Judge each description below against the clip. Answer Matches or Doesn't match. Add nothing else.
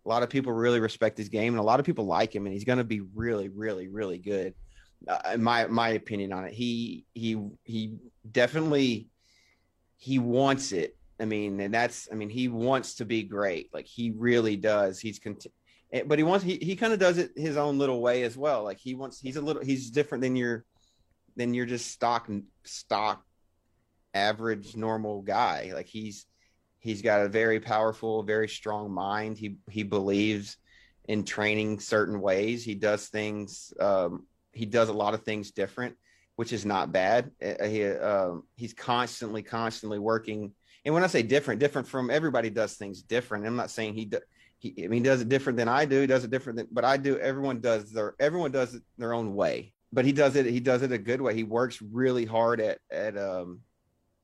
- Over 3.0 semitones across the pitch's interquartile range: Doesn't match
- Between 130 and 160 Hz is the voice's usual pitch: Doesn't match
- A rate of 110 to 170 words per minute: Doesn't match